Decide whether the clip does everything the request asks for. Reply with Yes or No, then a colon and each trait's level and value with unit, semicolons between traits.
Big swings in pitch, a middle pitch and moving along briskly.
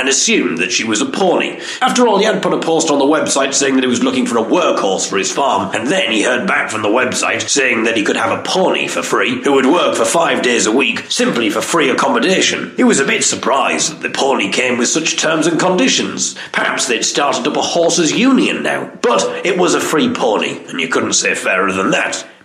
Yes: wide, 8.6 semitones; medium, 165 Hz; fast, 245 wpm